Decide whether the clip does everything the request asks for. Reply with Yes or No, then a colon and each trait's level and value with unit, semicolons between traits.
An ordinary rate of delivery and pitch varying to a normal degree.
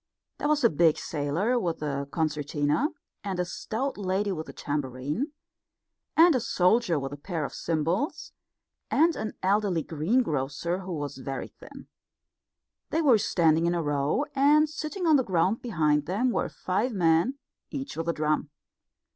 No: average, 160 wpm; wide, 8.1 semitones